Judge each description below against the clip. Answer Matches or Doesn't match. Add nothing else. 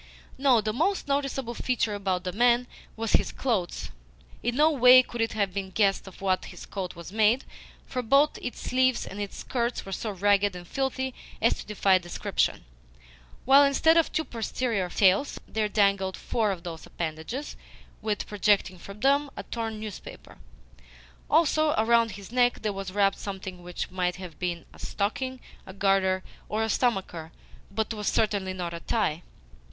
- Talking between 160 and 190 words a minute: Matches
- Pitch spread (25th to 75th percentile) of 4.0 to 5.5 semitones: Matches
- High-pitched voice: Matches